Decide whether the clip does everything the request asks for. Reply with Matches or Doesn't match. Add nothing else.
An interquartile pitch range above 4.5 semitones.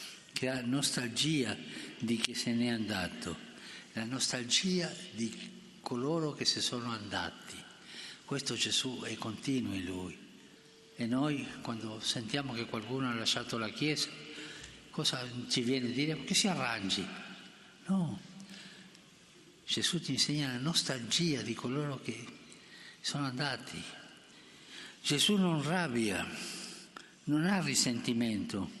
Matches